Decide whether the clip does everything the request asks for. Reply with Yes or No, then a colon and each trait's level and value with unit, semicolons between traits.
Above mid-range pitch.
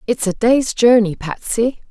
Yes: high, 225 Hz